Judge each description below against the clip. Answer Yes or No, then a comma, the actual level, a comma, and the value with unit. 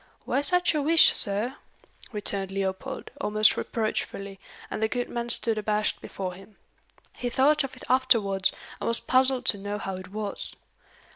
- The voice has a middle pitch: No, high, 215 Hz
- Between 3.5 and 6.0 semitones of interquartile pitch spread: Yes, average, 4.5 semitones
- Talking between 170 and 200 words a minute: No, average, 160 wpm